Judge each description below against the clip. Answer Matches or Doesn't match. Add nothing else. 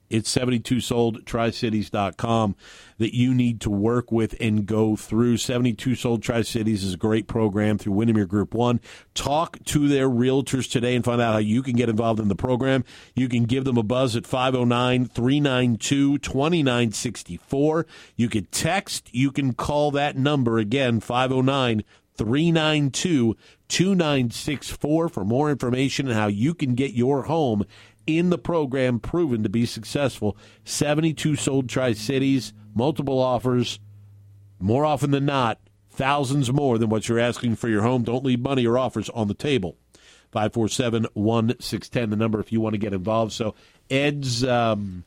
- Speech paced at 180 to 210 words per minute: Doesn't match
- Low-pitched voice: Matches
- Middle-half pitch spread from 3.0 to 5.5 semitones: Matches